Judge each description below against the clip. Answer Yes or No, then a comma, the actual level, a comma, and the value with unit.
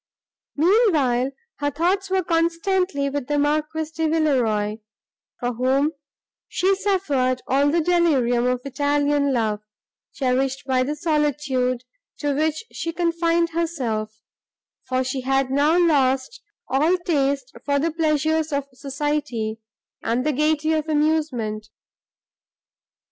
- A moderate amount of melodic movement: Yes, average, 3.8 semitones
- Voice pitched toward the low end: No, very high, 290 Hz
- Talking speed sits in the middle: No, slow, 120 wpm